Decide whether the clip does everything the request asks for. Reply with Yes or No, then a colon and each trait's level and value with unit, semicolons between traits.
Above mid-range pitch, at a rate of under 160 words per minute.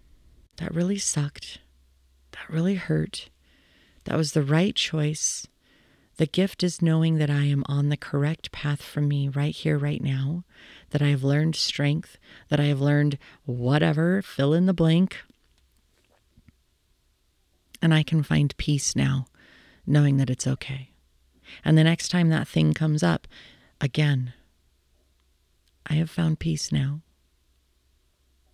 No: medium, 145 Hz; average, 140 wpm